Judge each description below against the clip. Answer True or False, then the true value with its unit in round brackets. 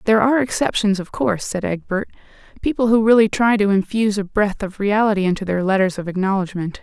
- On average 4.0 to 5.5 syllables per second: False (6.3 syllables/s)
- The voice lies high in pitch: True (200 Hz)